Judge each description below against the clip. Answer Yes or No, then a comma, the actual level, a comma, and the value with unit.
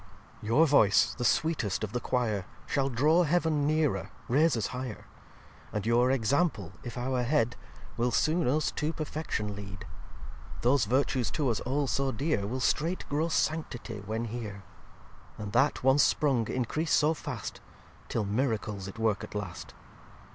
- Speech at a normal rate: Yes, average, 155 wpm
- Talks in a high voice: No, low, 125 Hz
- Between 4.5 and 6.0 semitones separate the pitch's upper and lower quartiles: Yes, wide, 5.4 semitones